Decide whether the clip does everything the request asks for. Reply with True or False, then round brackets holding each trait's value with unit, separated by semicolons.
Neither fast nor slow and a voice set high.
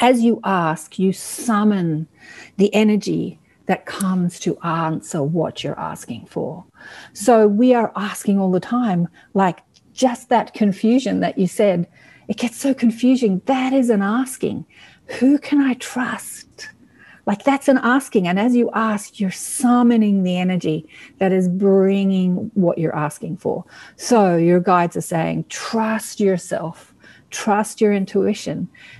True (145 wpm; 210 Hz)